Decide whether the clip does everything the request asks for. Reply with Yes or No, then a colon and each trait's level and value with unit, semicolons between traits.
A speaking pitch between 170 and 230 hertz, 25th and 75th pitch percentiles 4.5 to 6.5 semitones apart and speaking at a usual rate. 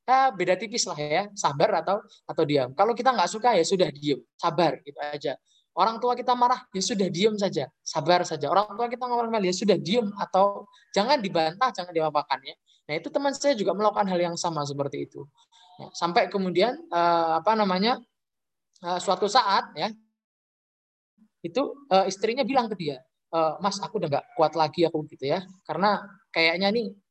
No: high, 190 Hz; average, 5.1 semitones; fast, 180 wpm